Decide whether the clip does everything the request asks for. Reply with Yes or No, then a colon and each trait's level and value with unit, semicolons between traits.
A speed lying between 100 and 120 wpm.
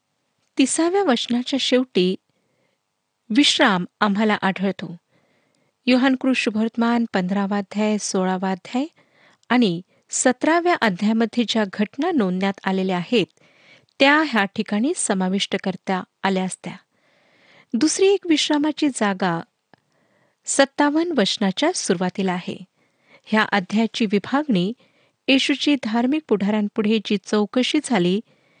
No: average, 90 wpm